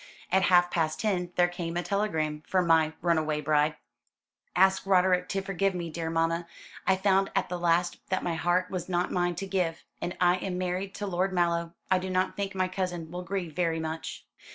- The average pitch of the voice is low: No, medium, 180 Hz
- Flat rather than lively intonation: Yes, narrow, 2.0 semitones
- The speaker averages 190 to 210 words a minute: Yes, average, 200 wpm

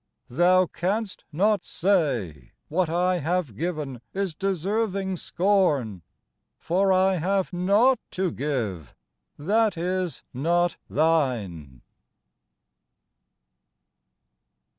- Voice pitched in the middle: Yes, medium, 175 Hz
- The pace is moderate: No, slow, 85 wpm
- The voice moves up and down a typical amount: Yes, average, 4.9 semitones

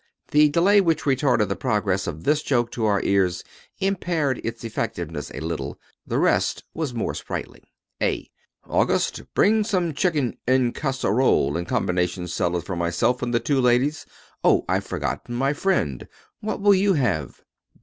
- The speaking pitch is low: Yes, low, 125 Hz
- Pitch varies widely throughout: Yes, wide, 8.9 semitones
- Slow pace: No, average, 160 wpm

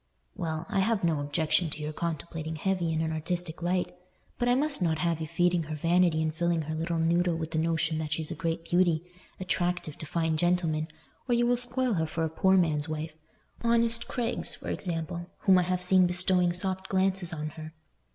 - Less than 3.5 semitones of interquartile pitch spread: Yes, narrow, 2.6 semitones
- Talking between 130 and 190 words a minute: No, average, 200 wpm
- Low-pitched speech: No, medium, 170 Hz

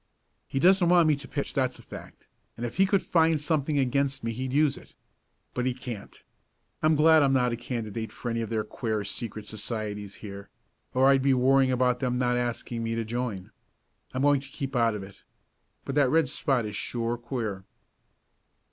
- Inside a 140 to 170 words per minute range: No, average, 200 wpm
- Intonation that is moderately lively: Yes, average, 3.4 semitones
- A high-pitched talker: No, low, 125 Hz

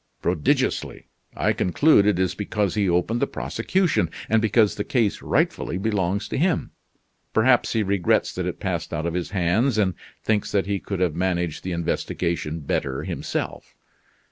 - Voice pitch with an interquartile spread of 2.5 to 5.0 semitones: Yes, average, 4.0 semitones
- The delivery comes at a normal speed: Yes, average, 165 wpm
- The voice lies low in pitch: Yes, low, 100 Hz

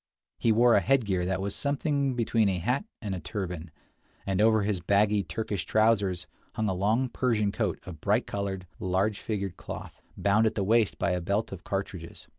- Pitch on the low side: Yes, low, 100 Hz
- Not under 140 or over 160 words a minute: No, average, 190 wpm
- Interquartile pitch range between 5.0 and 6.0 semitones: No, average, 3.0 semitones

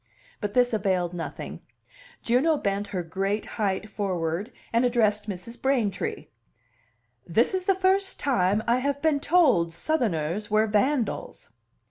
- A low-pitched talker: No, high, 215 Hz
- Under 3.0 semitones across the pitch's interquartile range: No, wide, 5.4 semitones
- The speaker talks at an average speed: No, slow, 130 wpm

